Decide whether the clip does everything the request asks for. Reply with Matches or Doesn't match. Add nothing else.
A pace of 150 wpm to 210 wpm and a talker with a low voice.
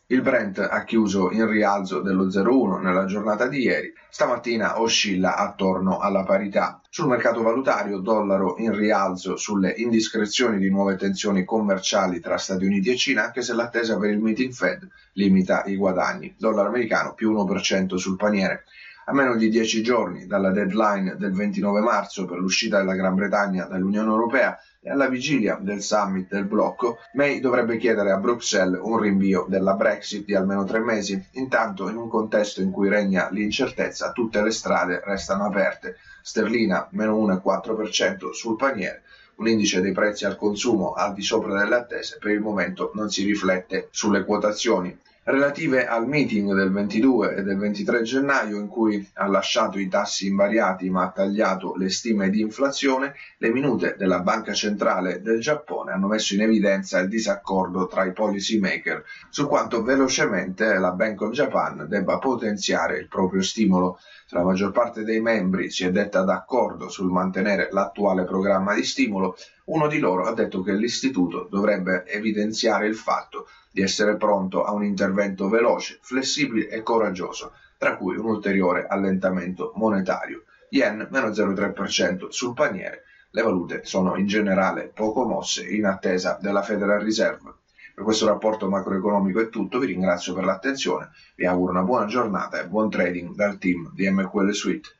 Matches